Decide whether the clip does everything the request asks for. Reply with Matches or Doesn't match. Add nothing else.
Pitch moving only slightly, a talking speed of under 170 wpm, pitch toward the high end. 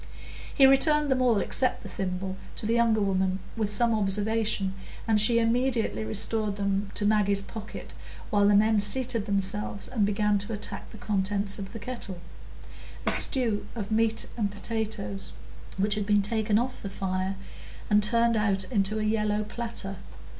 Matches